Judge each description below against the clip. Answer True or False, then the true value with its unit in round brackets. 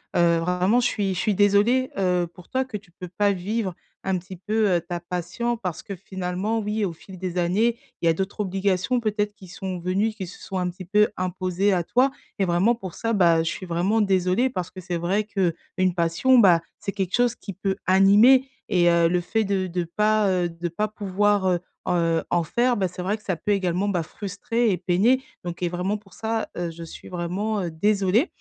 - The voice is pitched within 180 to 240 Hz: True (190 Hz)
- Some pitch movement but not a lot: True (3.0 semitones)